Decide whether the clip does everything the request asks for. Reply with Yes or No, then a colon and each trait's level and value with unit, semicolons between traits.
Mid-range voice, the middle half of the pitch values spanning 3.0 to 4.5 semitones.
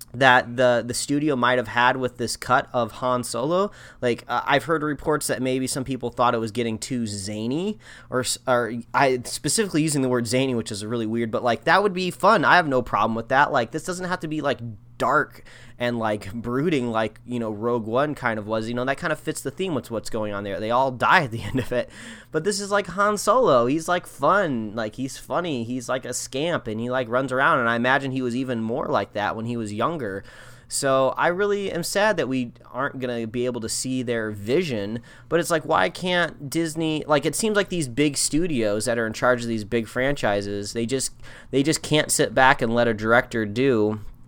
No: low, 125 Hz; average, 3.9 semitones